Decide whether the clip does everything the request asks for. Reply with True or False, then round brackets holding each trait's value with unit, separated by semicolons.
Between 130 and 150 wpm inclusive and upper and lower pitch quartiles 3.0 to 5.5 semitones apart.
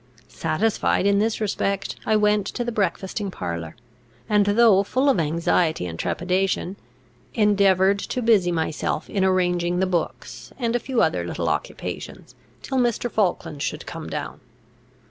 True (145 wpm; 3.7 semitones)